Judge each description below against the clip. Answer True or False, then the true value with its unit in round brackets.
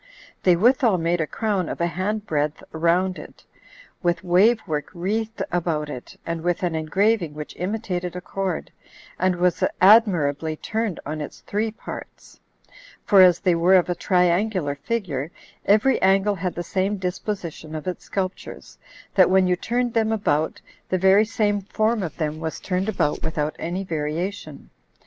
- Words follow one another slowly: False (165 wpm)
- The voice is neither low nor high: True (180 Hz)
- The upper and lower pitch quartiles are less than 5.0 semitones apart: True (3.8 semitones)